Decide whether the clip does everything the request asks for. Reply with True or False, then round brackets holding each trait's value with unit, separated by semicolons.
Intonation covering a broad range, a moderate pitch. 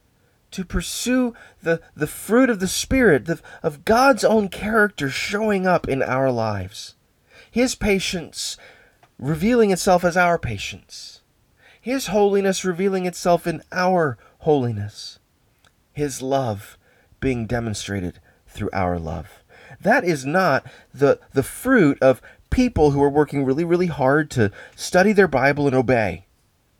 True (8.0 semitones; 150 Hz)